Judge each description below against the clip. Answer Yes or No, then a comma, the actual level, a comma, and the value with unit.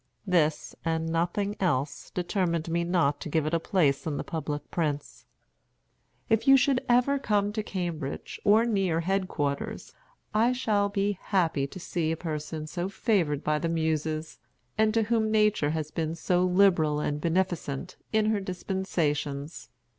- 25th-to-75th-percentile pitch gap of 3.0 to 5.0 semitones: Yes, average, 4.6 semitones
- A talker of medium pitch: Yes, medium, 175 Hz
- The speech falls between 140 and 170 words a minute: Yes, average, 160 wpm